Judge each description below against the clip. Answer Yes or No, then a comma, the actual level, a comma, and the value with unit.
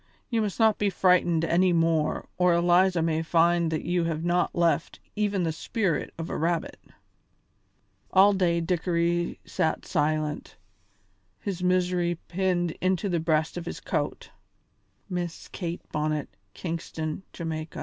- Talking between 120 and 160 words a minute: Yes, average, 140 wpm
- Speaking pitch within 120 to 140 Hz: No, medium, 175 Hz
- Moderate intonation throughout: No, narrow, 1.9 semitones